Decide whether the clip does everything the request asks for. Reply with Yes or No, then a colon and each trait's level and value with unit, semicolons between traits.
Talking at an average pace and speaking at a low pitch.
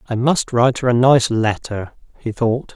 Yes: average, 195 wpm; low, 120 Hz